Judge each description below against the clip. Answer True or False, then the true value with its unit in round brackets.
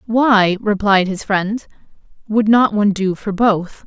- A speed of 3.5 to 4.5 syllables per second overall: True (3.9 syllables/s)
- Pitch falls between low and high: False (205 Hz)